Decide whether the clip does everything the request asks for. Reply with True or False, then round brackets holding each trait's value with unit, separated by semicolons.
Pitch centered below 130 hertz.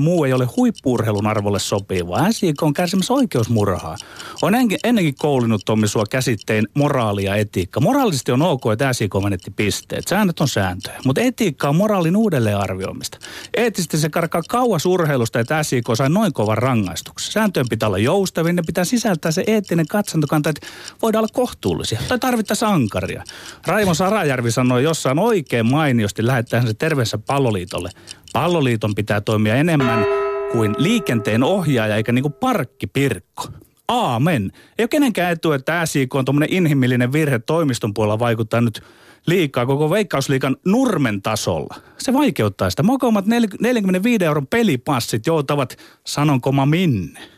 False (140 Hz)